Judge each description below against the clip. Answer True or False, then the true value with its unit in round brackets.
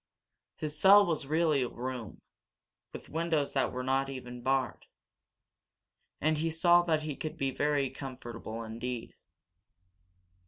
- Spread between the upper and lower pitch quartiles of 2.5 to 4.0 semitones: True (3.7 semitones)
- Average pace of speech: False (130 wpm)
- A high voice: False (135 Hz)